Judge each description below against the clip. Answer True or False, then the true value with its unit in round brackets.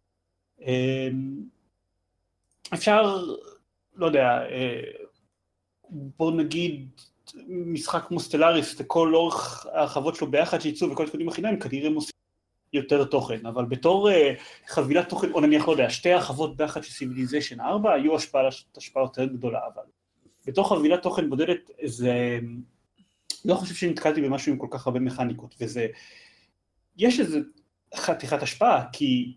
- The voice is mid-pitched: True (150 Hz)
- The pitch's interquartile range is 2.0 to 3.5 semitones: False (5.3 semitones)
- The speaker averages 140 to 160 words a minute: False (125 wpm)